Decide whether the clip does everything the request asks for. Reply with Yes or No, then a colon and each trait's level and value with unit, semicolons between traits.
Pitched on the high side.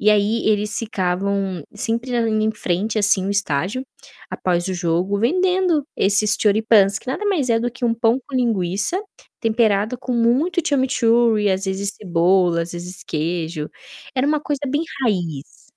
Yes: high, 210 Hz